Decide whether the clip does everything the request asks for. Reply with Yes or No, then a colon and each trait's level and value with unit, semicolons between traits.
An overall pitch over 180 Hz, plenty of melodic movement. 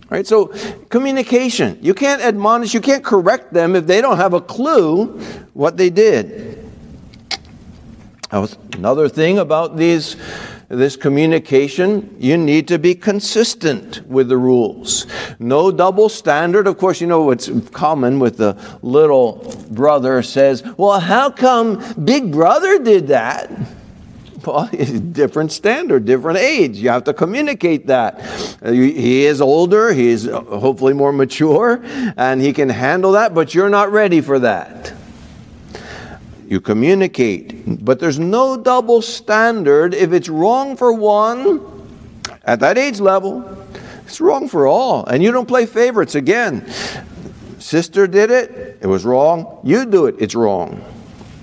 Yes: high, 190 Hz; wide, 8.2 semitones